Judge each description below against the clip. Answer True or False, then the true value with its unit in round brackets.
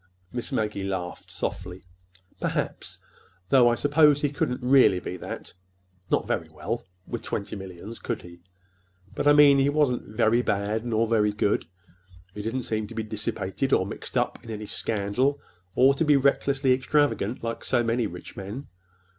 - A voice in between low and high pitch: False (110 Hz)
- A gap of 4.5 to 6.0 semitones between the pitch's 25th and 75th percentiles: True (5.4 semitones)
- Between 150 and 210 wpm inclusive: True (155 wpm)